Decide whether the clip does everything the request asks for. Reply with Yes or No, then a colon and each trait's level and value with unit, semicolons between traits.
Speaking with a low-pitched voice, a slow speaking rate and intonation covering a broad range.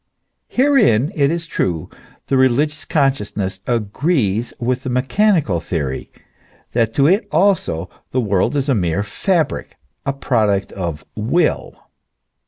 Yes: low, 125 Hz; slow, 125 wpm; wide, 7.2 semitones